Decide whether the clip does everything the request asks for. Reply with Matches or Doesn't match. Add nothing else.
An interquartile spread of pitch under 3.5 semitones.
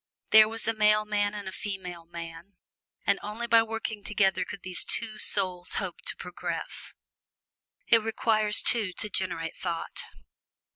Matches